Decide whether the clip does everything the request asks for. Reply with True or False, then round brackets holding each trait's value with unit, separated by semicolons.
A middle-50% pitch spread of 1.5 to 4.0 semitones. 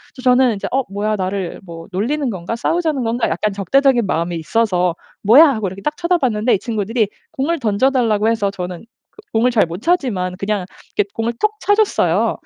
False (5.2 semitones)